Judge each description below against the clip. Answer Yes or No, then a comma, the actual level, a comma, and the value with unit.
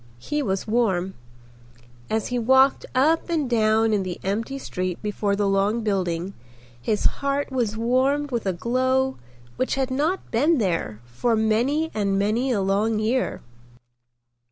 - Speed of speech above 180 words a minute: No, average, 150 wpm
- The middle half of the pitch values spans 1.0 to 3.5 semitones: No, average, 4.9 semitones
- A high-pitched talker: Yes, high, 225 Hz